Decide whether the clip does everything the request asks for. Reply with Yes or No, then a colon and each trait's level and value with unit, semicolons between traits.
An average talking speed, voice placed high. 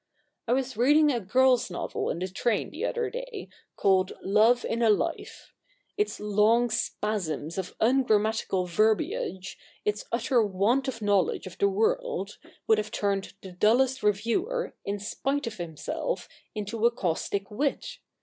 Yes: average, 150 wpm; high, 220 Hz